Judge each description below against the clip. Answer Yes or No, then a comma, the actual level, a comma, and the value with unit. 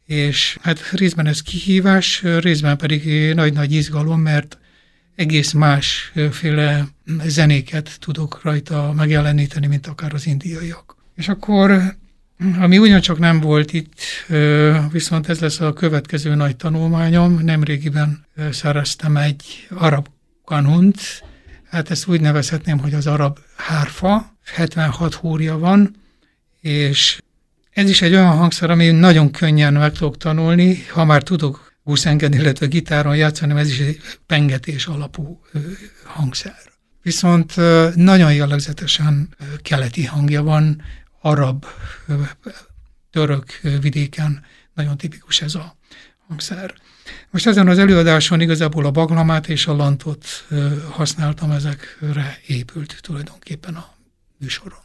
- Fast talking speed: No, average, 115 wpm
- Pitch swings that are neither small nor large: No, narrow, 2.3 semitones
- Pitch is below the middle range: No, medium, 155 Hz